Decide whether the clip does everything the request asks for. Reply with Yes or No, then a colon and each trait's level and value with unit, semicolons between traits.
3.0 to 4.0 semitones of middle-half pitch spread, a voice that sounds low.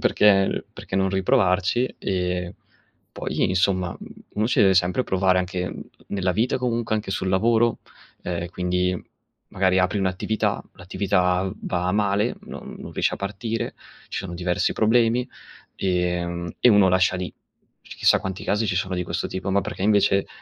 No: narrow, 2.4 semitones; very low, 95 Hz